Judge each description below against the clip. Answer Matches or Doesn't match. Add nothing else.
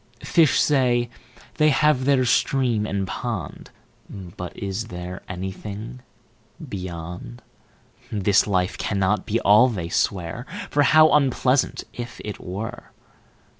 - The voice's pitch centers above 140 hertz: Doesn't match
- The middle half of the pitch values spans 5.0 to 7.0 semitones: Matches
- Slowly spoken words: Matches